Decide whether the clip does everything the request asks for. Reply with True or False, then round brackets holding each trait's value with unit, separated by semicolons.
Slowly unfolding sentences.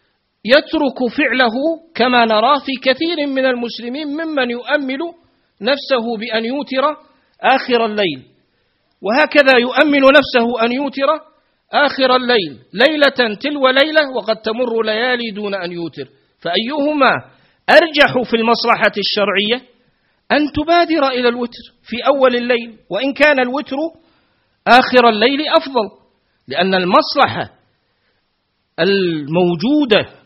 False (105 wpm)